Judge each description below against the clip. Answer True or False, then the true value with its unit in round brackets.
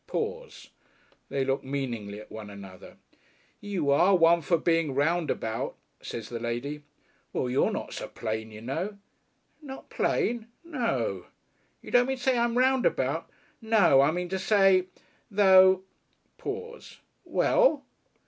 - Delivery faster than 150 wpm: False (140 wpm)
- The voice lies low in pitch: False (170 Hz)